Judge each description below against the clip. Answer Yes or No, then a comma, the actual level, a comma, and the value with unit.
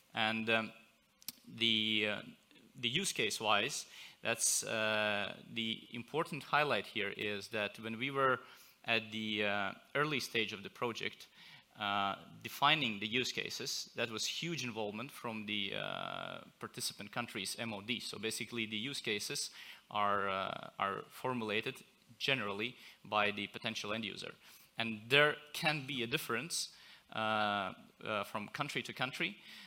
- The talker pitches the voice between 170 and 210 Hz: No, low, 115 Hz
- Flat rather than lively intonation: No, average, 3.1 semitones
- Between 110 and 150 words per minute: Yes, average, 140 wpm